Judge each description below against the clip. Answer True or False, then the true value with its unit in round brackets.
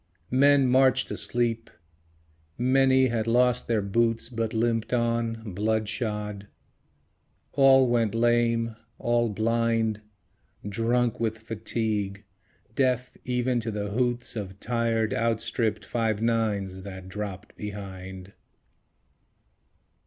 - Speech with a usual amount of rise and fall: False (2.3 semitones)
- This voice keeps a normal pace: False (100 wpm)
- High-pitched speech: False (115 Hz)